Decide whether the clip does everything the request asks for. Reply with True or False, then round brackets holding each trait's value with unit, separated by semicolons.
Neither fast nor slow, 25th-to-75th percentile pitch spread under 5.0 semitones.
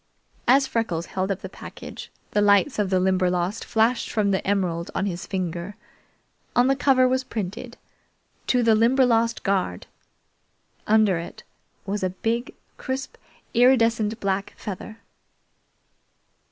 False (130 wpm; 3.8 semitones)